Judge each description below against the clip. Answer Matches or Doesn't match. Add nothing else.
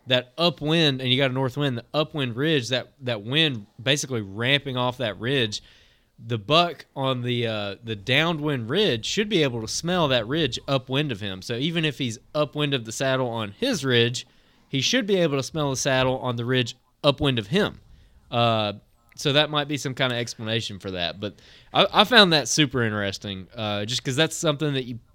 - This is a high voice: Doesn't match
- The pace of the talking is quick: Matches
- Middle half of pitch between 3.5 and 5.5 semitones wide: Matches